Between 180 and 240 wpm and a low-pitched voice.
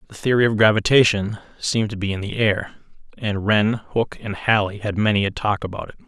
Yes: fast, 205 wpm; low, 105 Hz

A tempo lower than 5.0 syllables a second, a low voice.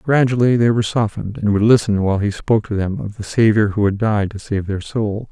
No: 5.9 syllables/s; low, 105 Hz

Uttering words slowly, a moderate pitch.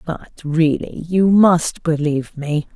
Yes: slow, 130 wpm; medium, 160 Hz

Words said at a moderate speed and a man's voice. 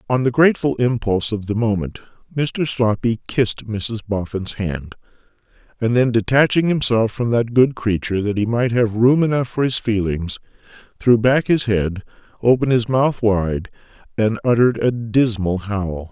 Yes: average, 160 wpm; male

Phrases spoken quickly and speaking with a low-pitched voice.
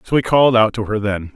Yes: fast, 310 wpm; low, 110 Hz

